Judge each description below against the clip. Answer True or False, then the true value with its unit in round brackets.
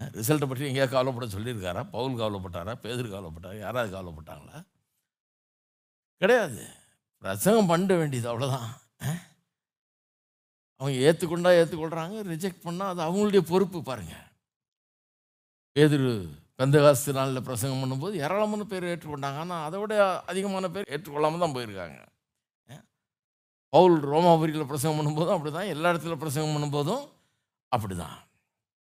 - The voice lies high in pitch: False (150 Hz)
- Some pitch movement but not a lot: False (5.7 semitones)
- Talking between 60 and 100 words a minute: False (110 wpm)